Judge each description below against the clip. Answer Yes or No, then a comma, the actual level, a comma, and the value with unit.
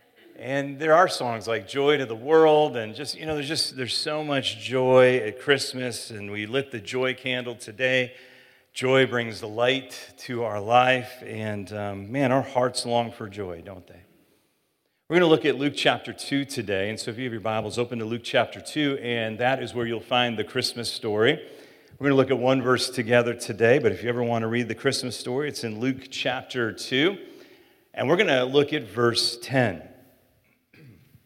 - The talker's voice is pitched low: Yes, low, 125 Hz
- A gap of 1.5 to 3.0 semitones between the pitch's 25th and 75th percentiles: Yes, narrow, 2.5 semitones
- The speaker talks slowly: No, fast, 205 wpm